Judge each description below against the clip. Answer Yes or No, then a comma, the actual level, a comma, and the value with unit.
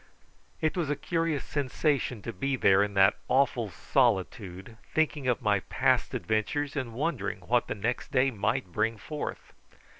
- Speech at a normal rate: Yes, average, 155 wpm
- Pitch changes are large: Yes, wide, 5.7 semitones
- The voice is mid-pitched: No, low, 125 Hz